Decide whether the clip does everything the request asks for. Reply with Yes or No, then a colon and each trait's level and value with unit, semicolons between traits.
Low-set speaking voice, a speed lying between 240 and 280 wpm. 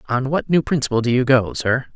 Yes: low, 125 Hz; fast, 245 wpm